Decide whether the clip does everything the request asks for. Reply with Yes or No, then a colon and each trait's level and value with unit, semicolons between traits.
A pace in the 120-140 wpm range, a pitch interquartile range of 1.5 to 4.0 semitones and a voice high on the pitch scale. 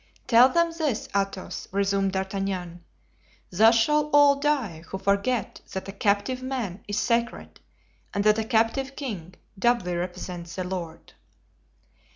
No: slow, 135 wpm; average, 5.1 semitones; high, 205 Hz